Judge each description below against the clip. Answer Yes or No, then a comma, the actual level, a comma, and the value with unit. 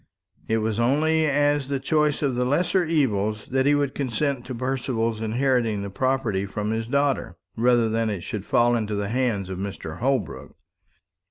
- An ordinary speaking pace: Yes, average, 175 wpm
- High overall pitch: No, low, 120 Hz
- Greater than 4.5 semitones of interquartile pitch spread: No, average, 4.2 semitones